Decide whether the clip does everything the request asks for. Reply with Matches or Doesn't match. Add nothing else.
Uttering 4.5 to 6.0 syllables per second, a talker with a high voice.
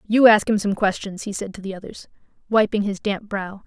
Matches